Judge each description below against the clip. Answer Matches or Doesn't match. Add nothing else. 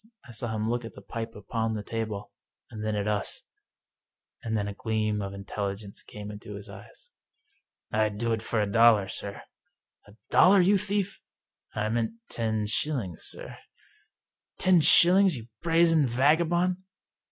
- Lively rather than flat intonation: Matches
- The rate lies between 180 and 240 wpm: Doesn't match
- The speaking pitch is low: Matches